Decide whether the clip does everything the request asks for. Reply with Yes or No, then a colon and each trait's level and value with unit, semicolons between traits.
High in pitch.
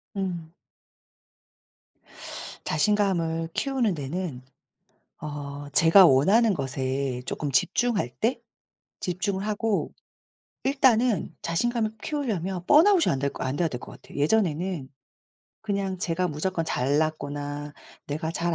No: medium, 170 Hz